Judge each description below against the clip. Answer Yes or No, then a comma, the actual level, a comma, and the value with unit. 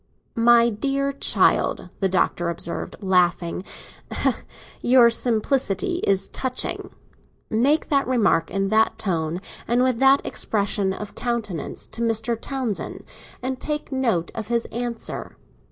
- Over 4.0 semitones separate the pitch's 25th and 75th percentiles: Yes, average, 4.8 semitones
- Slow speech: Yes, slow, 125 wpm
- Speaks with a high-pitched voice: Yes, high, 230 Hz